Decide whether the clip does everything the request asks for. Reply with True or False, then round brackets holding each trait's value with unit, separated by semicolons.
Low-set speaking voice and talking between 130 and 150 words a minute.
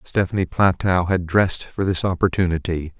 True (90 Hz; 140 wpm)